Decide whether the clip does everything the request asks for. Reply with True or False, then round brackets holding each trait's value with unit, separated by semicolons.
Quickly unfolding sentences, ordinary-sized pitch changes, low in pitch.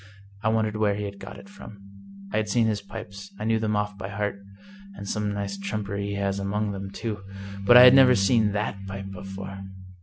False (220 wpm; 1.9 semitones; 105 Hz)